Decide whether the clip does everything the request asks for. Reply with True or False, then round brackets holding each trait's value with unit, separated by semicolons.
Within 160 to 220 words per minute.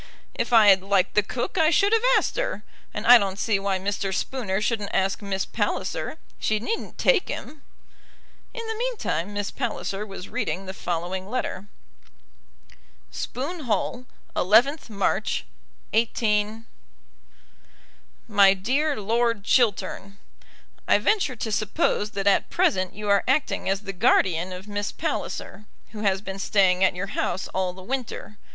False (150 wpm)